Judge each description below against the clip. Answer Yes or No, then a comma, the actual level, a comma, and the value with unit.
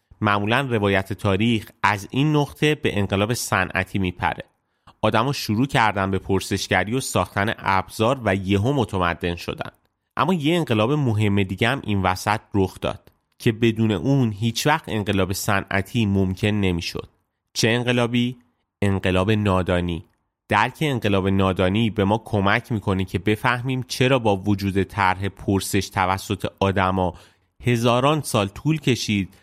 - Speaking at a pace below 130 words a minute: No, average, 135 wpm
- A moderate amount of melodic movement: Yes, average, 3.6 semitones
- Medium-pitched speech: No, low, 105 Hz